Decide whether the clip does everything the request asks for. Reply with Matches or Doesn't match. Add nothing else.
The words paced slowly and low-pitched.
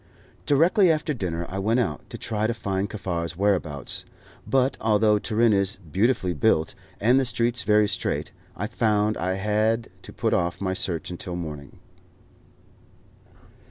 Doesn't match